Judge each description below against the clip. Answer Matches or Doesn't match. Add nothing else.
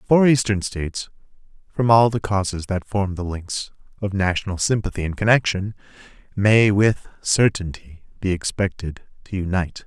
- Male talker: Matches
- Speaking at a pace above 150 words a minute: Doesn't match